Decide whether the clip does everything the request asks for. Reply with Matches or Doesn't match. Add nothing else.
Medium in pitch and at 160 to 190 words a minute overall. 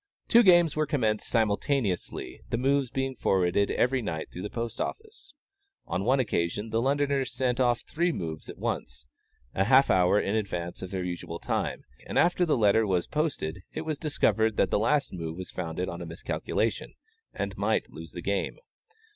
Doesn't match